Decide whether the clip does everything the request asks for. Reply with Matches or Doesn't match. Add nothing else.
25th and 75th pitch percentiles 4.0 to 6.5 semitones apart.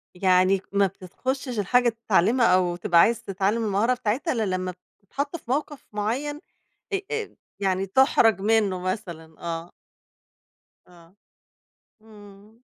Matches